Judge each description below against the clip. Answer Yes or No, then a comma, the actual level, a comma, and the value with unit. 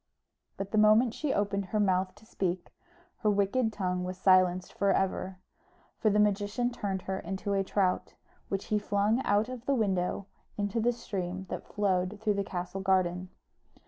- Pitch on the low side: No, high, 200 Hz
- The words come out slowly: No, average, 175 wpm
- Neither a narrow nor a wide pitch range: No, narrow, 2.3 semitones